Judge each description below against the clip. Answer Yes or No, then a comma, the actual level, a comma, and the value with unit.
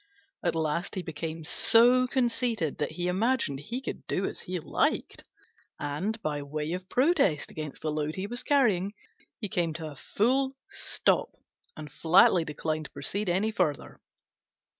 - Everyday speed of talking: Yes, average, 160 wpm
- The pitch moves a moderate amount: No, wide, 6.8 semitones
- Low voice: No, medium, 180 Hz